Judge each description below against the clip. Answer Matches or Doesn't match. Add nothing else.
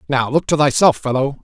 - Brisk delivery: Matches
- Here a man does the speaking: Matches